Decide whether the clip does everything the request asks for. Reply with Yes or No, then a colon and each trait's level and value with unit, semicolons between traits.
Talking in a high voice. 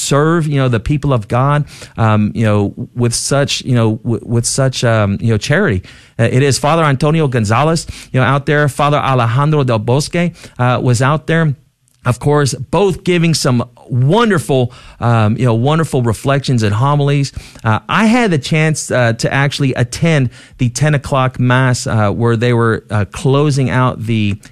No: low, 130 Hz